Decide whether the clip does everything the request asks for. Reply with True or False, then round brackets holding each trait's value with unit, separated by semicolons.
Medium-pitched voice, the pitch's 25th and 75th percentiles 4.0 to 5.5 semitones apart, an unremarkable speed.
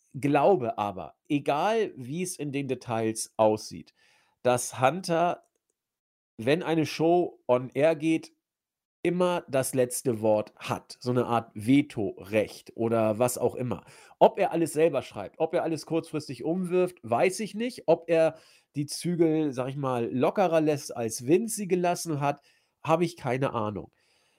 True (145 Hz; 5.2 semitones; 150 wpm)